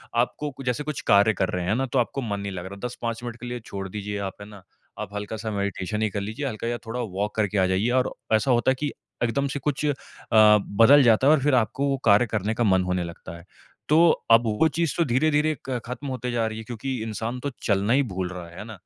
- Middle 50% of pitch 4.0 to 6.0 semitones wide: Yes, average, 4.3 semitones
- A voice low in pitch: Yes, low, 115 Hz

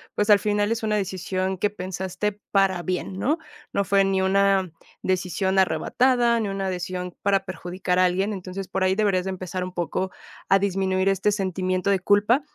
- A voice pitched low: No, high, 190 Hz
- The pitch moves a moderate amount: No, narrow, 1.5 semitones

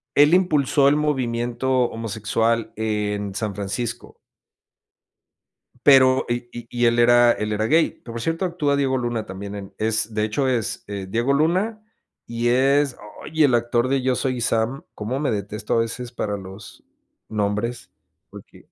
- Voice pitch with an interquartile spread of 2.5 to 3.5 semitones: No, average, 3.9 semitones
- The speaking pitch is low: Yes, low, 120 Hz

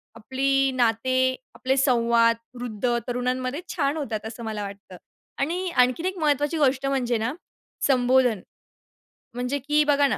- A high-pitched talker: Yes, very high, 255 Hz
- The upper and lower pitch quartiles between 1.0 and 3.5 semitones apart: Yes, average, 2.9 semitones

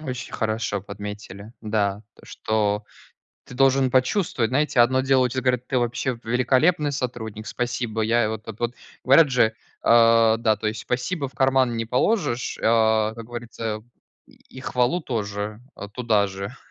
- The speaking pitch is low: Yes, low, 115 Hz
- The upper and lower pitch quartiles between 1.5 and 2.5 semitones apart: No, average, 2.9 semitones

